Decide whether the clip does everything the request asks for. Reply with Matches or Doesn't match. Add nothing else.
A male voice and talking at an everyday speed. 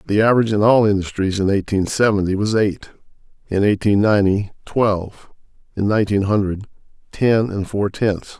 Matches